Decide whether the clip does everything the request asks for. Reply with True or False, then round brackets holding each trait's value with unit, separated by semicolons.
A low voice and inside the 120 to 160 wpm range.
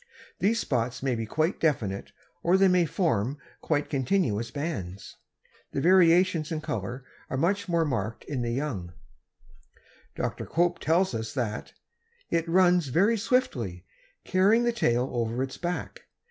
False (150 Hz; 145 wpm)